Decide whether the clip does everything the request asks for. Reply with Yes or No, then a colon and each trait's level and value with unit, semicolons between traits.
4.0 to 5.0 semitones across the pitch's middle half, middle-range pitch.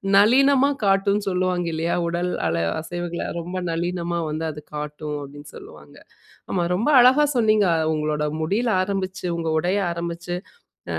No: average, 3.6 semitones; medium, 175 Hz